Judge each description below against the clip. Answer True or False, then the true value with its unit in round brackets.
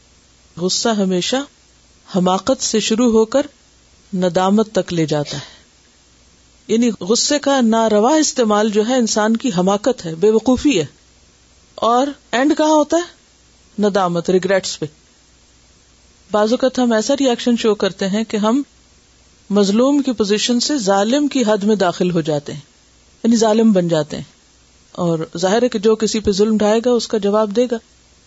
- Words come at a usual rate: True (145 wpm)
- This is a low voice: False (215 Hz)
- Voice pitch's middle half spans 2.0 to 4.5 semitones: False (5.6 semitones)